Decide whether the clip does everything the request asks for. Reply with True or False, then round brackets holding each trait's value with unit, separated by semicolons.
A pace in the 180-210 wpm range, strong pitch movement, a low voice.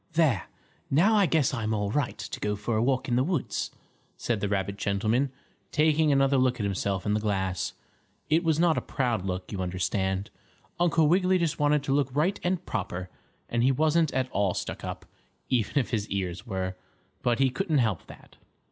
True (195 wpm; 6.9 semitones; 125 Hz)